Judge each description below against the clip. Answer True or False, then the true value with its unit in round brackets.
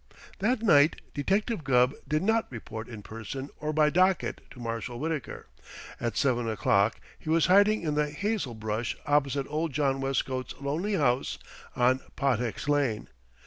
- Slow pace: False (150 wpm)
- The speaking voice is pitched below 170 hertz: True (140 Hz)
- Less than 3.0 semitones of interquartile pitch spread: False (4.8 semitones)